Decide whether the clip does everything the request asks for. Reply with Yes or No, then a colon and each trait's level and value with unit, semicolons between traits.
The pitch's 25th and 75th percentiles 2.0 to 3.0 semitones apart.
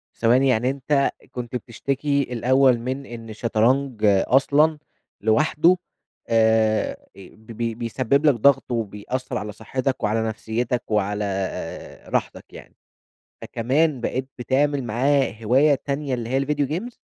No: average, 3.6 semitones